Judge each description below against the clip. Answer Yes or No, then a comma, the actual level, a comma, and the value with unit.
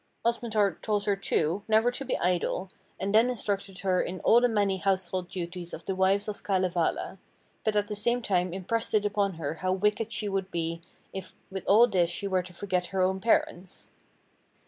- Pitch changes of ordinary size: No, narrow, 2.3 semitones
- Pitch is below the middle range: No, high, 195 Hz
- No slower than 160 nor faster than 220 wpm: Yes, average, 195 wpm